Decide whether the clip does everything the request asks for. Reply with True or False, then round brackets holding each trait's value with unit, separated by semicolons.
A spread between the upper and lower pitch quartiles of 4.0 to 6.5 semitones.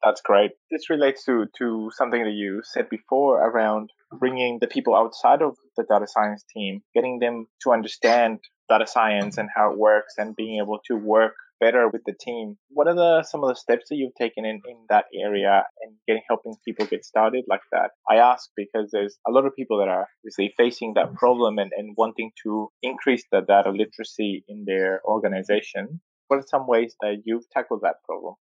False (3.0 semitones)